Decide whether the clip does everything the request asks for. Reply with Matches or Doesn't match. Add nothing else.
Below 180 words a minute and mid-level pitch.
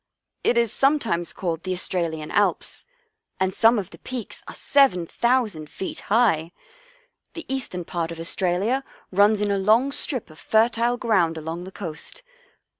Doesn't match